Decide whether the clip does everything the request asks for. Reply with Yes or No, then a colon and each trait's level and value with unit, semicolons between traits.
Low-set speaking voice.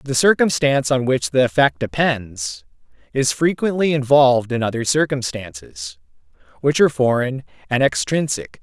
Yes: low, 125 Hz